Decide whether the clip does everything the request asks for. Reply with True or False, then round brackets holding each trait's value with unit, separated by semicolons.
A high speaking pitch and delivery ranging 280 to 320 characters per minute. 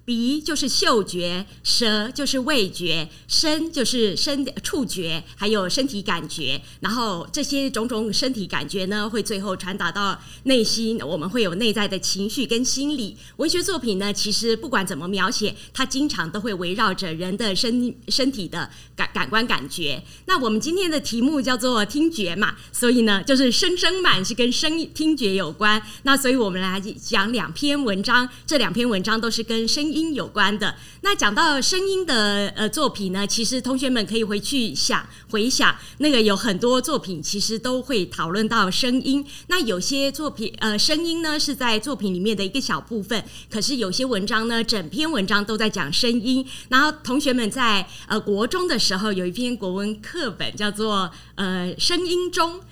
False (225 Hz; 270 characters per minute)